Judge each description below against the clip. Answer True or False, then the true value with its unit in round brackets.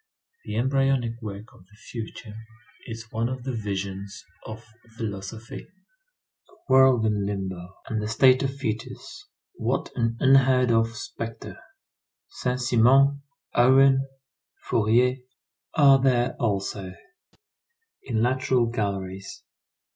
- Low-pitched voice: True (115 Hz)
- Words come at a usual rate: False (110 wpm)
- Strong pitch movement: False (3.7 semitones)